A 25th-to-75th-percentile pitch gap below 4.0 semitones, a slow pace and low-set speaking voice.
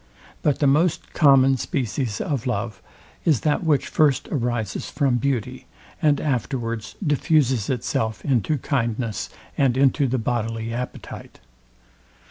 Yes: average, 3.6 semitones; slow, 120 wpm; low, 130 Hz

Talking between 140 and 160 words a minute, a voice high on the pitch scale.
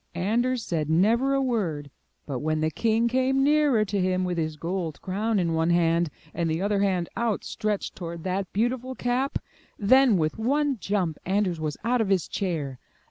No: average, 185 wpm; high, 195 Hz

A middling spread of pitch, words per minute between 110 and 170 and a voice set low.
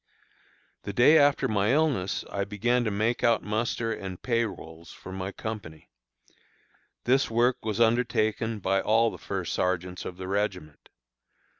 Yes: average, 3.8 semitones; average, 150 wpm; low, 110 Hz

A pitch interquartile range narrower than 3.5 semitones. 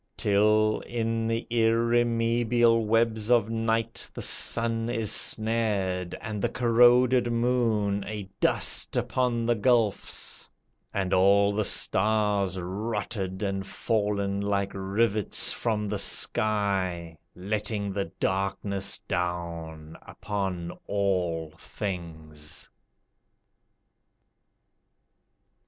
Yes: average, 2.9 semitones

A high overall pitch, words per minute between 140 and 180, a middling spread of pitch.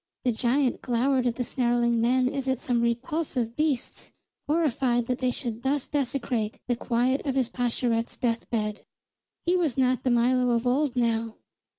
No: very high, 250 Hz; average, 170 wpm; narrow, 2.0 semitones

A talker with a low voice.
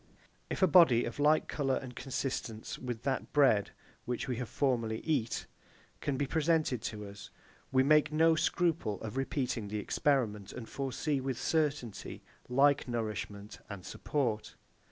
Yes: low, 130 Hz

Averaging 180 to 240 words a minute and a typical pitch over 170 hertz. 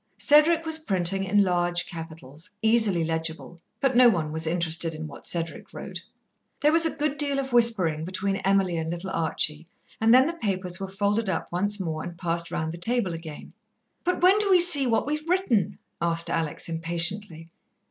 Yes: average, 185 wpm; medium, 185 Hz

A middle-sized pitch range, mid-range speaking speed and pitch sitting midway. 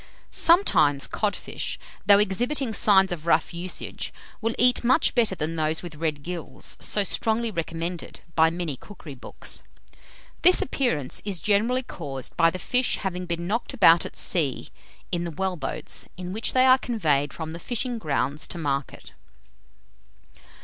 No: wide, 5.7 semitones; average, 155 wpm; medium, 180 Hz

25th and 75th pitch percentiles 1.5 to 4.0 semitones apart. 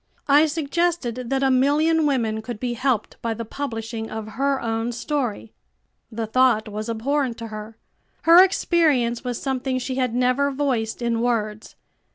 Yes: average, 3.7 semitones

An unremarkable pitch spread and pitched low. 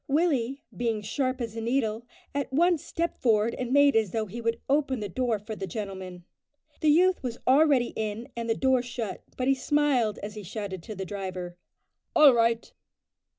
No: average, 4.3 semitones; high, 235 Hz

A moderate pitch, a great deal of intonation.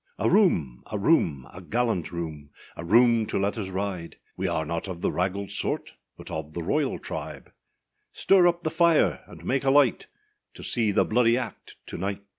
No: low, 100 Hz; wide, 6.9 semitones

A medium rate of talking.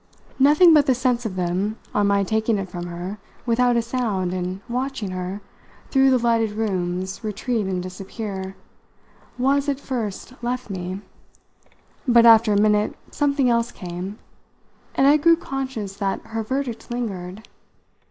Yes: average, 150 wpm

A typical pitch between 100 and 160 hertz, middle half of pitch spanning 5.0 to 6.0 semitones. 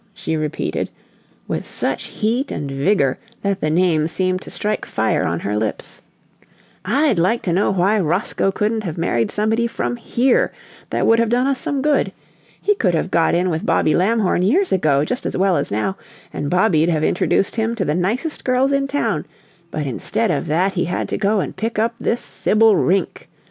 No: high, 190 Hz; wide, 5.6 semitones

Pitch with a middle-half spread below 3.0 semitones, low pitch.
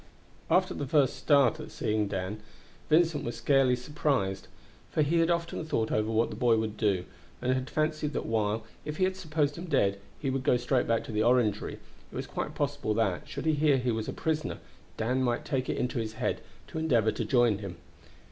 No: wide, 5.4 semitones; low, 125 Hz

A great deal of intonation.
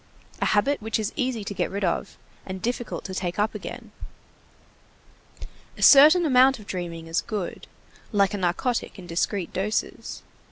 No: average, 4.8 semitones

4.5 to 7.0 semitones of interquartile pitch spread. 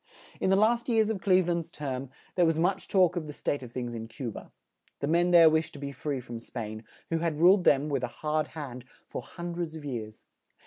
Yes: average, 5.2 semitones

